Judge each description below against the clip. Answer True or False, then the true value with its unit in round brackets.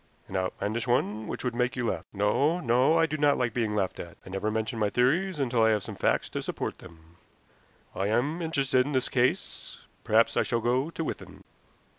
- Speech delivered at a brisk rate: True (210 wpm)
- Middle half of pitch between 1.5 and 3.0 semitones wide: False (4.4 semitones)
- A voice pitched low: True (120 Hz)